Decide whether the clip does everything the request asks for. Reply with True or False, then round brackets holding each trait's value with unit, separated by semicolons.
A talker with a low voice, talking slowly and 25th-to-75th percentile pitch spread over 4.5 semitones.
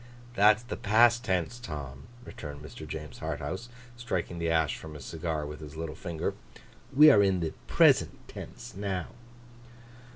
False (85 Hz; 155 wpm; 5.2 semitones)